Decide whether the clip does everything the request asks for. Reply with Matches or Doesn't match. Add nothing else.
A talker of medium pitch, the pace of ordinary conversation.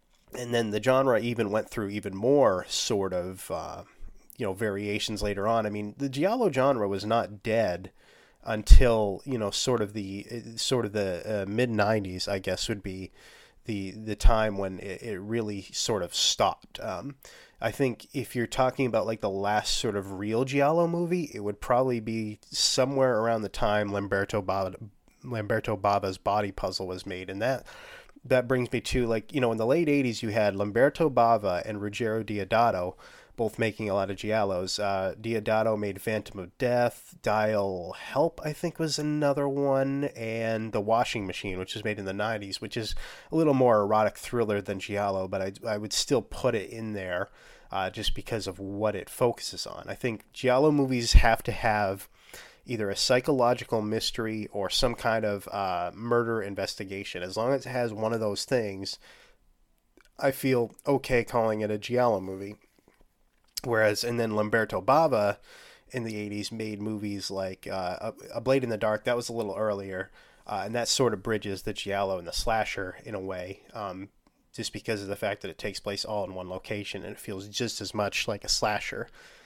Doesn't match